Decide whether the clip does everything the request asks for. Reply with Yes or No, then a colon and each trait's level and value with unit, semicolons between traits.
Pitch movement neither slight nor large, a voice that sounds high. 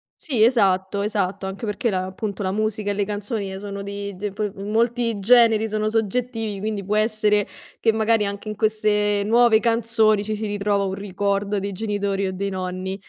No: narrow, 1.7 semitones; high, 205 Hz